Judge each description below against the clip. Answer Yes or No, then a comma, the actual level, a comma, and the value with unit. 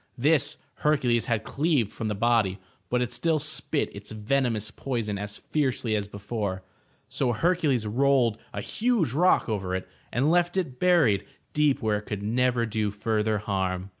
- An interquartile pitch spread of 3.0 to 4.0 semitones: No, average, 5.1 semitones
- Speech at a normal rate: Yes, average, 165 wpm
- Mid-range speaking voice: No, low, 115 Hz